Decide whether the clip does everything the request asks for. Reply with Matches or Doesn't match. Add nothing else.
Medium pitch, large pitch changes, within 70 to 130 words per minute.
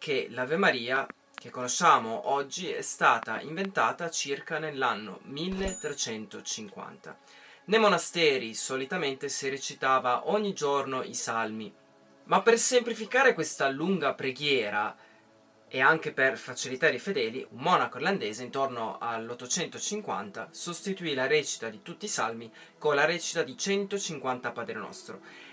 Matches